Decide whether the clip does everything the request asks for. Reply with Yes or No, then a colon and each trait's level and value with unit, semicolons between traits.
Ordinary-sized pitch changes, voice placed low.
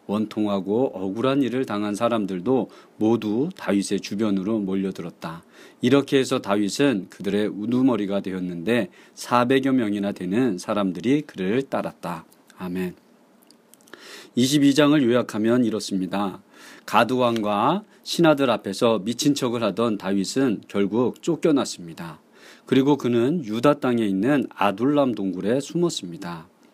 Yes: average, 4.8 semitones; low, 110 Hz